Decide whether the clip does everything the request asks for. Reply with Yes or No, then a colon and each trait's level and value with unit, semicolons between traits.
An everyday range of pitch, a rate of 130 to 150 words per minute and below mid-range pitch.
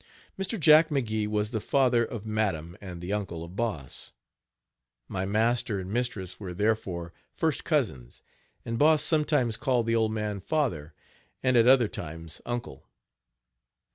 Yes: average, 5.0 semitones; average, 145 wpm; low, 110 Hz